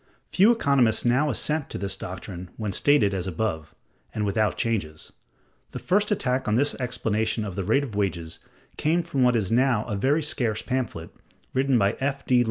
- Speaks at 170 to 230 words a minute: Yes, average, 180 wpm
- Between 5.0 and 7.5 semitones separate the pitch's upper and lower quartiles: Yes, wide, 5.6 semitones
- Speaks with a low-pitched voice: Yes, low, 115 Hz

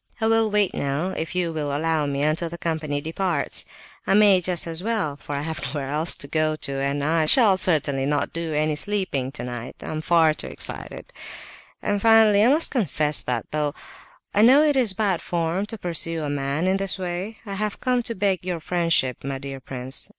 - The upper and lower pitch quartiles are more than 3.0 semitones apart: Yes, average, 5.3 semitones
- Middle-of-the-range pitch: Yes, medium, 165 Hz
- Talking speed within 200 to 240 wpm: Yes, fast, 205 wpm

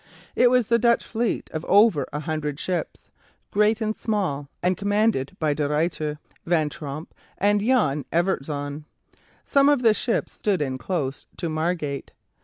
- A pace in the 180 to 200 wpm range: No, average, 155 wpm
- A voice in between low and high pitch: Yes, medium, 170 Hz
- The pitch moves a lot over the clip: Yes, wide, 6.4 semitones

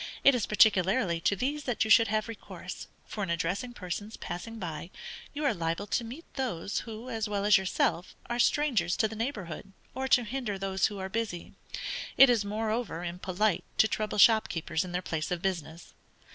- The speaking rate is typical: Yes, average, 185 wpm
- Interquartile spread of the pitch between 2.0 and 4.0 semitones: No, average, 4.4 semitones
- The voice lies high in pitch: Yes, high, 210 Hz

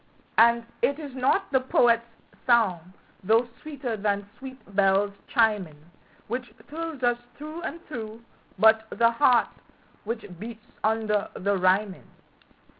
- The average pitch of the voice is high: Yes, high, 230 Hz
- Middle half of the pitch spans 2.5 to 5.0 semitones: Yes, average, 3.7 semitones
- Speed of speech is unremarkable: No, slow, 125 wpm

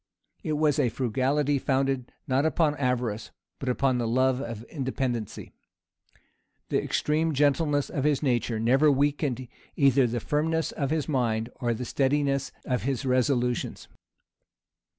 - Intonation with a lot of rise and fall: No, average, 2.9 semitones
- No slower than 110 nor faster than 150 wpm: Yes, slow, 135 wpm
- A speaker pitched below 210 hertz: Yes, low, 135 Hz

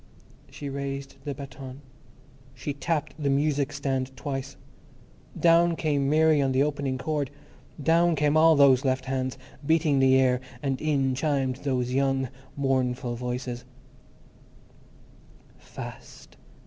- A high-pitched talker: No, medium, 140 Hz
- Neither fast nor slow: No, slow, 120 wpm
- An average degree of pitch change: No, narrow, 2.0 semitones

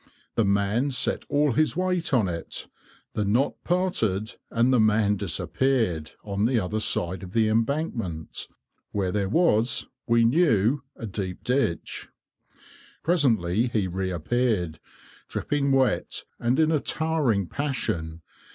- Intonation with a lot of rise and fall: Yes, wide, 5.8 semitones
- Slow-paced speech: Yes, slow, 130 wpm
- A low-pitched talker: Yes, low, 115 Hz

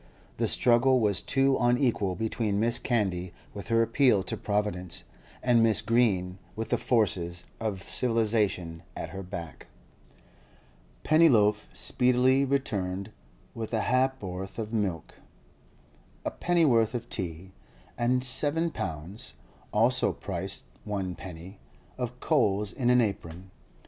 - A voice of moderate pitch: No, low, 110 Hz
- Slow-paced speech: Yes, slow, 120 wpm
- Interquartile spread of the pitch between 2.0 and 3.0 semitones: No, average, 4.6 semitones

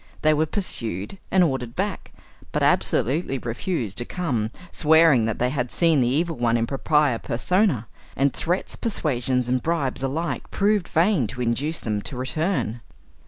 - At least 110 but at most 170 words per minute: Yes, average, 160 wpm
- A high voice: No, low, 135 Hz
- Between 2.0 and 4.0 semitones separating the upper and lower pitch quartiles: No, wide, 5.6 semitones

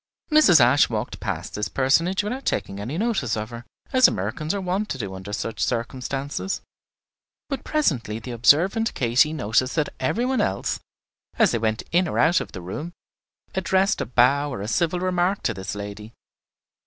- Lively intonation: Yes, wide, 8.8 semitones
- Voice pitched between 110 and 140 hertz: Yes, low, 135 Hz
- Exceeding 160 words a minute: Yes, average, 180 wpm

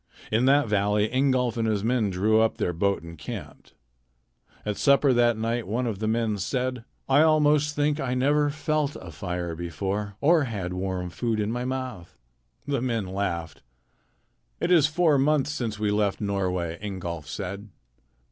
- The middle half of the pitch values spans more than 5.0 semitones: Yes, wide, 5.5 semitones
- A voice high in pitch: No, low, 110 Hz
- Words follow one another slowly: No, average, 165 wpm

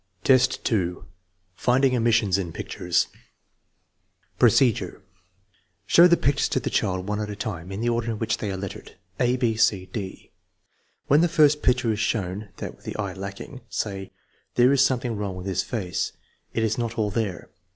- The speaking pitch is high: No, low, 110 Hz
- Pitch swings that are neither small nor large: Yes, average, 4.2 semitones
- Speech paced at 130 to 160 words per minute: No, average, 180 wpm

